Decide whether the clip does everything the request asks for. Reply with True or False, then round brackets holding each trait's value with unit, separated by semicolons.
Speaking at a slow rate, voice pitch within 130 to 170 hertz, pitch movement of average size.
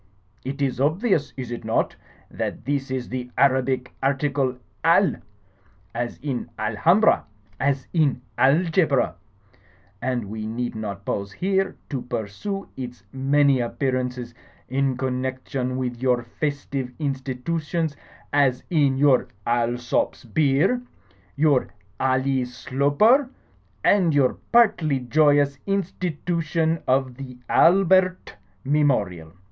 True (110 wpm; 135 Hz; 3.5 semitones)